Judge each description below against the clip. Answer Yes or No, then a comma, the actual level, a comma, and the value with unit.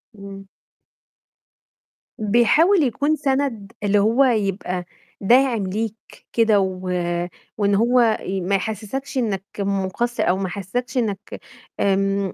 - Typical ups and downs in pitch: Yes, average, 3.7 semitones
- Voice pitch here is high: Yes, high, 210 Hz